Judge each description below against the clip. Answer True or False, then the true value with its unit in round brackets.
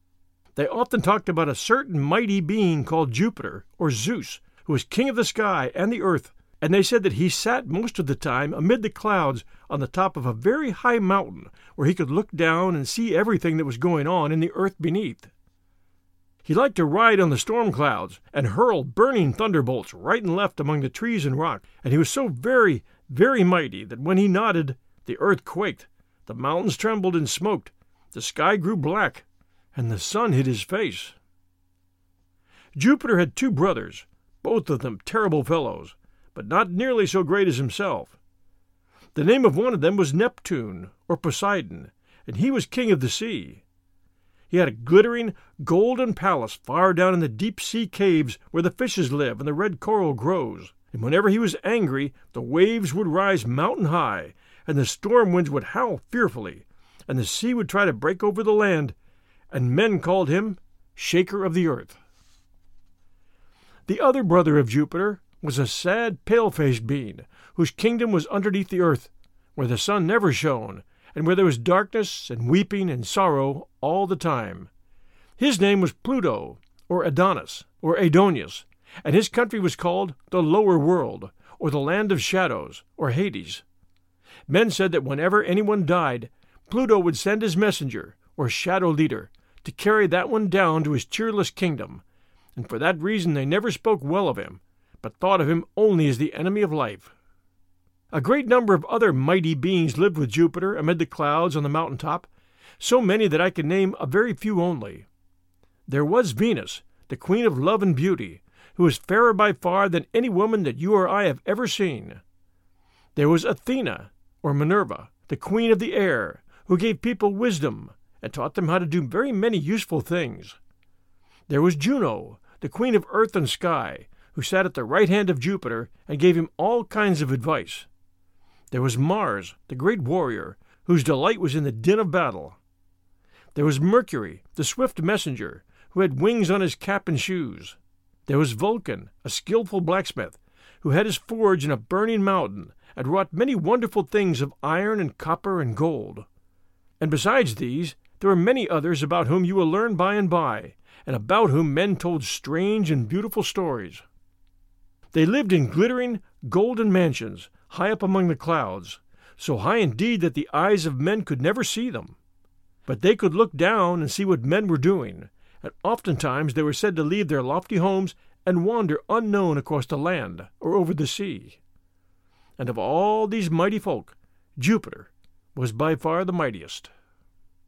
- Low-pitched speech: False (170 Hz)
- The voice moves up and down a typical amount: False (7.9 semitones)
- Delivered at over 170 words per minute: True (180 wpm)